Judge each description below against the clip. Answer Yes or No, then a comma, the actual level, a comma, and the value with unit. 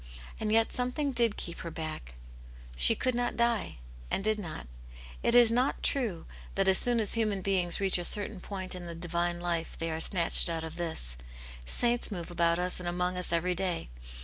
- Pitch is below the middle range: No, medium, 180 Hz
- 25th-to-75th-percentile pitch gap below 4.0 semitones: No, average, 4.5 semitones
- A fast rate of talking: Yes, fast, 215 wpm